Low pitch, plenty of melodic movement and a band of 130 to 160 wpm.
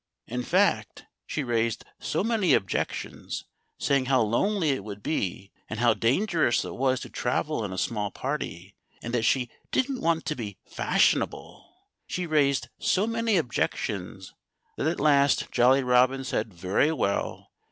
Yes: low, 130 Hz; wide, 5.9 semitones; average, 150 wpm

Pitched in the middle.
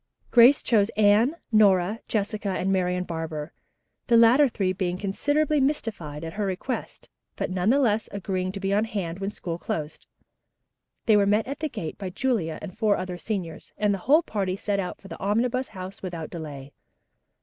No: high, 200 Hz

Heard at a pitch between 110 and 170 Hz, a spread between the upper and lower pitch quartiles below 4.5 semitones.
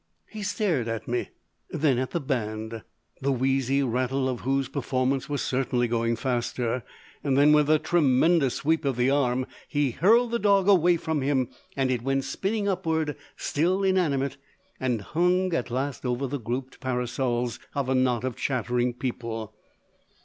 Yes: low, 135 Hz; average, 4.0 semitones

